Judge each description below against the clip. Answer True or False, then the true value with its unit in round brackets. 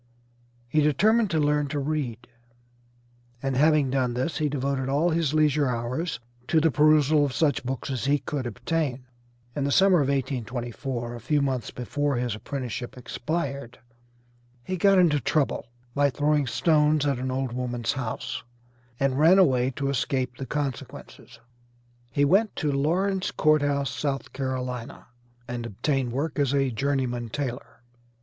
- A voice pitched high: False (140 Hz)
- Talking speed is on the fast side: False (155 wpm)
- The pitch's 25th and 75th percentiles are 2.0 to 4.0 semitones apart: True (3.1 semitones)